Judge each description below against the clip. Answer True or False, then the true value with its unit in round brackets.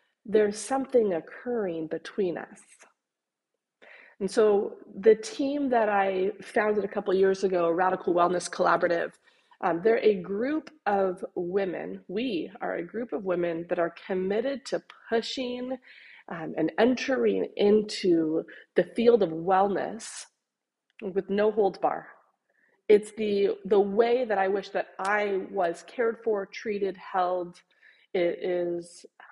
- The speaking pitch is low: False (200 Hz)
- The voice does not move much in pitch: False (4.0 semitones)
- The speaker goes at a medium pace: False (130 wpm)